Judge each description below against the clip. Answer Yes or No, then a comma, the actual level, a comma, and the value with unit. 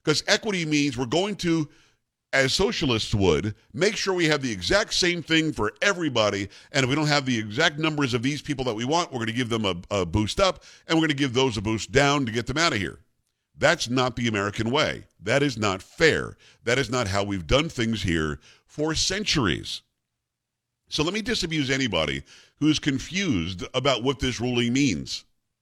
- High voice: No, low, 135 Hz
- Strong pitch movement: Yes, wide, 5.7 semitones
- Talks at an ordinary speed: No, fast, 210 wpm